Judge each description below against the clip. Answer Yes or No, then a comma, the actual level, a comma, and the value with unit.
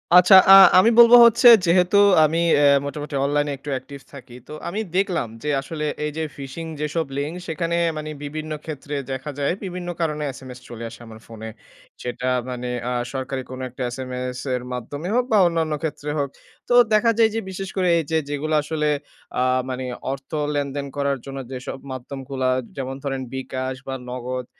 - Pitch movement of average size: Yes, average, 3.8 semitones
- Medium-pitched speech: Yes, medium, 145 Hz